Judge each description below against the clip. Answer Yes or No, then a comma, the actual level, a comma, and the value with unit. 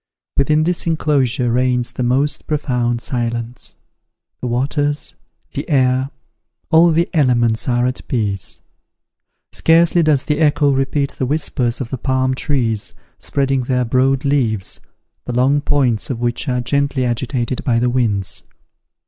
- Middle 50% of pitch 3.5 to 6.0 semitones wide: No, average, 3.0 semitones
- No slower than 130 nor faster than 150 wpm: Yes, average, 140 wpm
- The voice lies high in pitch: No, low, 130 Hz